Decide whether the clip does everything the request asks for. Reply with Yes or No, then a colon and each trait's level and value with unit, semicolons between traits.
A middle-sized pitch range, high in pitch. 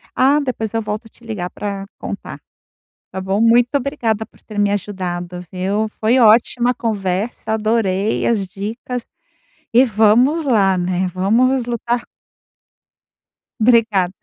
Yes: average, 3.6 semitones; high, 220 Hz